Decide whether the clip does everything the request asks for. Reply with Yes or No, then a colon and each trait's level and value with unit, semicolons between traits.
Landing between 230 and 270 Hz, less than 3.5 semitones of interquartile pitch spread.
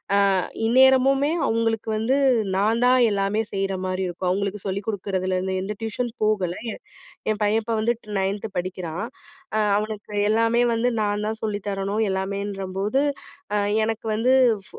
No: high, 210 Hz; narrow, 2.5 semitones